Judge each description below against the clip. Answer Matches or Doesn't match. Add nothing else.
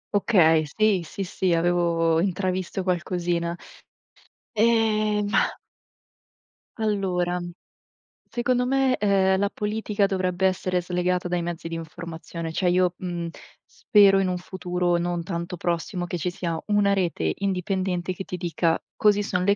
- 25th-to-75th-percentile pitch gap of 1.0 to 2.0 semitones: Doesn't match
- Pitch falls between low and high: Matches